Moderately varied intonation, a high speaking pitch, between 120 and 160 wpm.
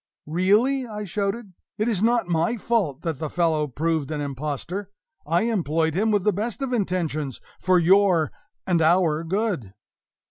No: average, 4.9 semitones; medium, 180 Hz; average, 155 wpm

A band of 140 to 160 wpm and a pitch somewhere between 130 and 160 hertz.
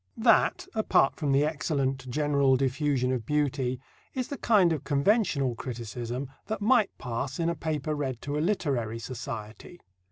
Yes: average, 155 wpm; medium, 140 Hz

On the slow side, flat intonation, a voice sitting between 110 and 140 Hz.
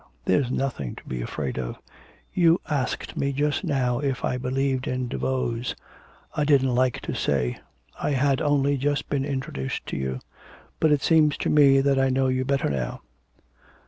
No: average, 175 wpm; narrow, 2.1 semitones; low, 135 Hz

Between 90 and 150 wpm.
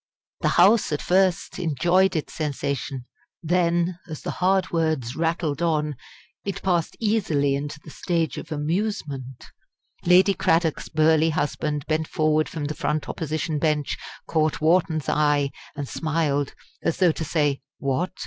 Yes: average, 140 wpm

